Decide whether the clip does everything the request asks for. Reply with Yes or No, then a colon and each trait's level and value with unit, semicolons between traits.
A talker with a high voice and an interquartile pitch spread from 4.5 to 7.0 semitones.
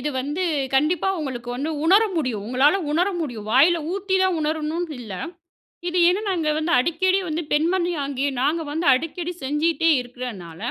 Yes: very high, 310 Hz; average, 4.8 semitones